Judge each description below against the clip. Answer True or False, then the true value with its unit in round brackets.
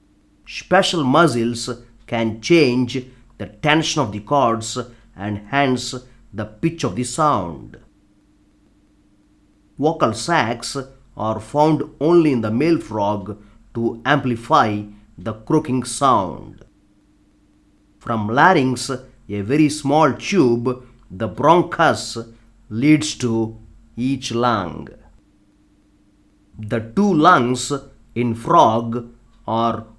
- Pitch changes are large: False (4.4 semitones)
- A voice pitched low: True (115 Hz)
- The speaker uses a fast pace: False (95 wpm)